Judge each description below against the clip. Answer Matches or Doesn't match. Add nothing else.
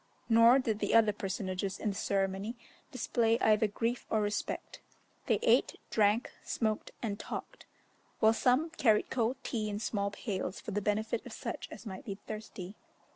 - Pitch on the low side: Doesn't match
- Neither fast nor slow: Matches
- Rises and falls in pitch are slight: Matches